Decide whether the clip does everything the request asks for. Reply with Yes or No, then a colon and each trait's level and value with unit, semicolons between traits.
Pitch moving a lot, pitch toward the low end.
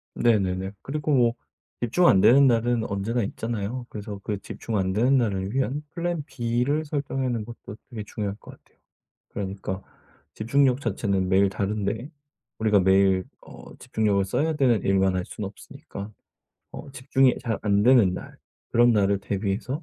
No: average, 4.5 semitones; low, 110 Hz